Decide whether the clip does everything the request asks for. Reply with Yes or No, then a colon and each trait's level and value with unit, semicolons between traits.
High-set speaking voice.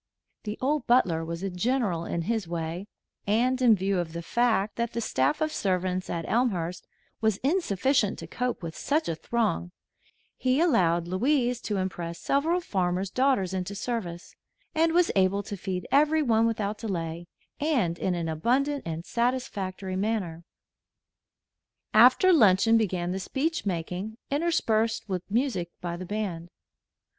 Yes: high, 205 Hz